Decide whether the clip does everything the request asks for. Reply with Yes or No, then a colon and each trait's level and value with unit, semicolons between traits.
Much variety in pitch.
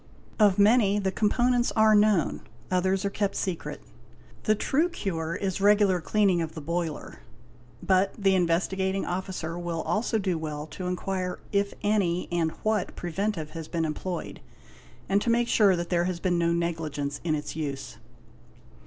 No: average, 3.4 semitones